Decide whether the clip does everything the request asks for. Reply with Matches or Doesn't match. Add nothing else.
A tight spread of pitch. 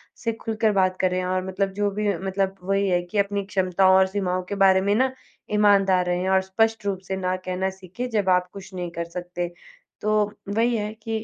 Matches